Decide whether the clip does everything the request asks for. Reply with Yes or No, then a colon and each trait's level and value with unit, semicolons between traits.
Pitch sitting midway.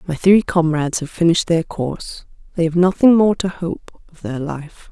Yes: medium, 170 Hz